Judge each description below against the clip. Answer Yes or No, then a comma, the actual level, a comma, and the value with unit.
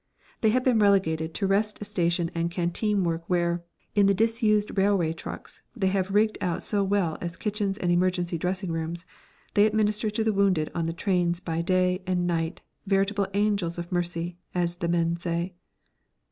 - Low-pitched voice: No, medium, 185 Hz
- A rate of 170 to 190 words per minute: Yes, average, 175 wpm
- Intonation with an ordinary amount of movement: Yes, average, 3.1 semitones